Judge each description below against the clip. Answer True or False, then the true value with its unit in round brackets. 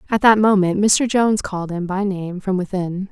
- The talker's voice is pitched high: True (195 Hz)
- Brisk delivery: True (210 wpm)